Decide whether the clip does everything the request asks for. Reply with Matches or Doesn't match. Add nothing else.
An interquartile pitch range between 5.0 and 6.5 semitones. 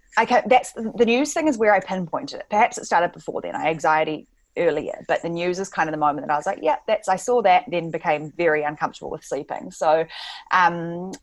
Matches